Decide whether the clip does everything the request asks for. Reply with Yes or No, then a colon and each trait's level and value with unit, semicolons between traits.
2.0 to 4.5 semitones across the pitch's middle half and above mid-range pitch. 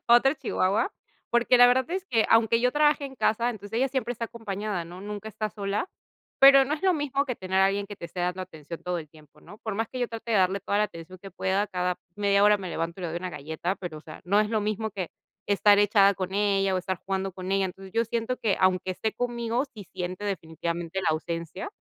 Yes: average, 3.9 semitones; high, 200 Hz